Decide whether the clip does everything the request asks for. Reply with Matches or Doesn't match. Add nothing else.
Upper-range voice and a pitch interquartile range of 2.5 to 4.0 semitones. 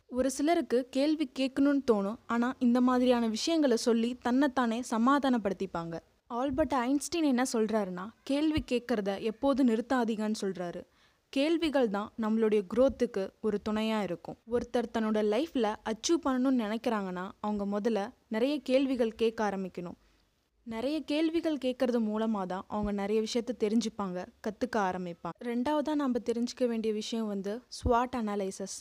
Matches